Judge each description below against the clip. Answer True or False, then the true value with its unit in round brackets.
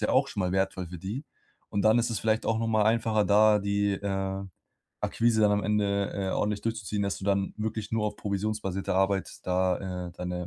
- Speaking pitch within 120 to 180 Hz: False (100 Hz)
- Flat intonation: True (2.0 semitones)